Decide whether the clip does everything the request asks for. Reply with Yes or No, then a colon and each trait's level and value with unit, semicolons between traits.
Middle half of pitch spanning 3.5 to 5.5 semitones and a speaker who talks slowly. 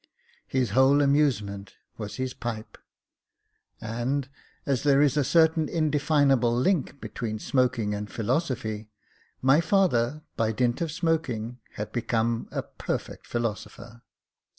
Yes: average, 4.2 semitones; slow, 120 wpm